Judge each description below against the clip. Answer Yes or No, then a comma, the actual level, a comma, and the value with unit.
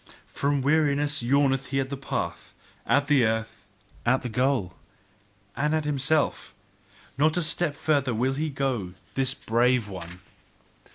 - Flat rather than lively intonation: No, average, 3.2 semitones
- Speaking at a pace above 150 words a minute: No, average, 145 wpm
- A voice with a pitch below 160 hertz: Yes, low, 135 Hz